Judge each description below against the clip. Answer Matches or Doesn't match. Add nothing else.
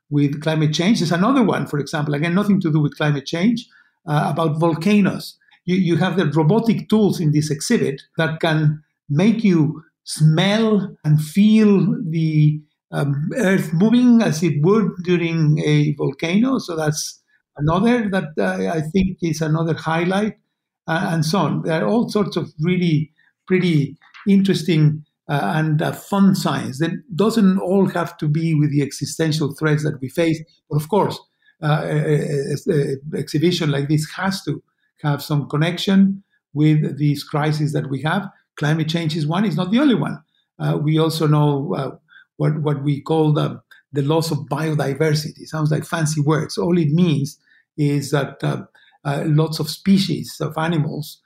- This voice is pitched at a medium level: Matches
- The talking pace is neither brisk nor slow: Matches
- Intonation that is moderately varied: Matches